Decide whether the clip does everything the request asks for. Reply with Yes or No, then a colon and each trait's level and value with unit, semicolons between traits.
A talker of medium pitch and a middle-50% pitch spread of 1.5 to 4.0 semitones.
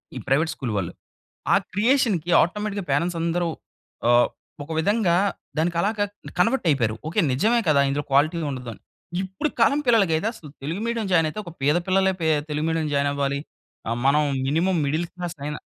No: medium, 165 Hz; average, 5.1 semitones